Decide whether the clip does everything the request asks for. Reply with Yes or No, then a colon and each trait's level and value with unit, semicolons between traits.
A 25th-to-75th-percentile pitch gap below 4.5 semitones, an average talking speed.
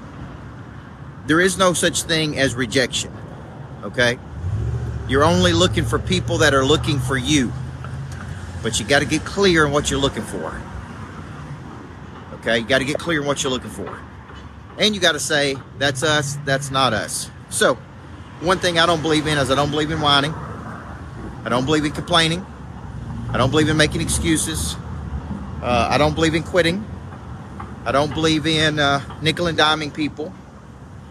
No: average, 5.1 semitones; average, 170 wpm